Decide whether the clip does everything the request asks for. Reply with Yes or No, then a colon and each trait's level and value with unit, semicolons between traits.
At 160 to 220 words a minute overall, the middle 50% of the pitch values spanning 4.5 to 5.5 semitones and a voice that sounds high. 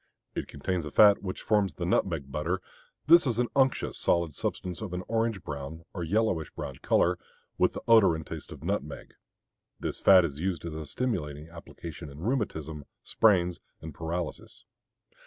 No: average, 170 wpm; average, 4.9 semitones; very low, 85 Hz